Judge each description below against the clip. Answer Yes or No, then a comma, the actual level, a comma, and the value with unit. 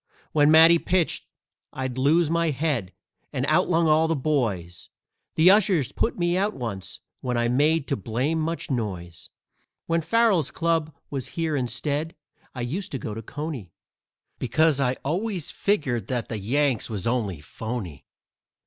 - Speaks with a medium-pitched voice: Yes, medium, 145 Hz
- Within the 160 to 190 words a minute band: No, average, 150 wpm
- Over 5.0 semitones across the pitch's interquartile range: Yes, wide, 5.6 semitones